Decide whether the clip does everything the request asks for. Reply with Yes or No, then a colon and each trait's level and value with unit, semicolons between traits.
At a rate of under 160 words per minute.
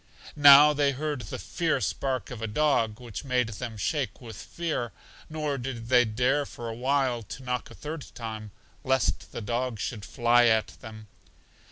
No: average, 175 wpm